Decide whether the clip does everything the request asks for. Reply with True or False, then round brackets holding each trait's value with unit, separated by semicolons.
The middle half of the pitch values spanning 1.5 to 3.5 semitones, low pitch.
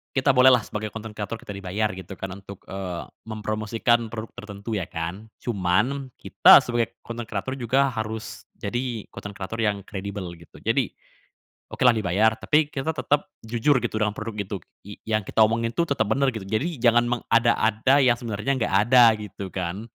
True (2.9 semitones; 110 Hz)